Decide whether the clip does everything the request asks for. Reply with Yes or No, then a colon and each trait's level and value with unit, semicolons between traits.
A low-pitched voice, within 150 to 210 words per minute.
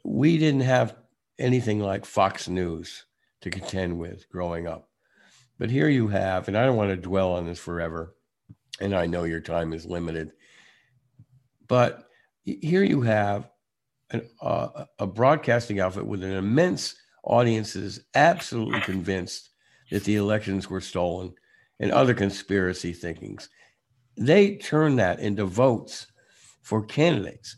No: low, 100 Hz; slow, 135 wpm